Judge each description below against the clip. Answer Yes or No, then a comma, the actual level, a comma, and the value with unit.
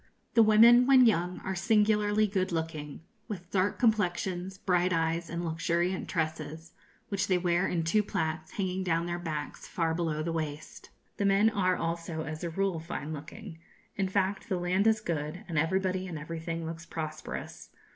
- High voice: No, medium, 175 Hz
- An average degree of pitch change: Yes, average, 3.2 semitones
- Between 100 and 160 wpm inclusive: No, average, 170 wpm